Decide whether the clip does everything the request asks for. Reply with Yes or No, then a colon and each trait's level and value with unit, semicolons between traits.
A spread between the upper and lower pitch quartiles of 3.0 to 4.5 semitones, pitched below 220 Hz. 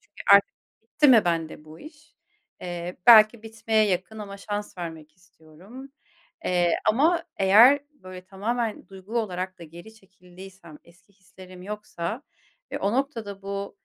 Yes: average, 3.7 semitones; high, 195 Hz